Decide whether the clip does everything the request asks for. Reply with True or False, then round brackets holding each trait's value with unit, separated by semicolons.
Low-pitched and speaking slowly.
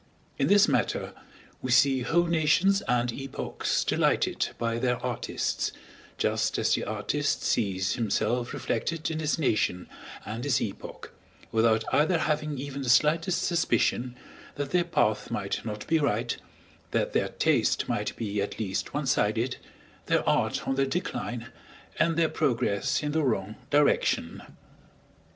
False (130 Hz; 145 wpm)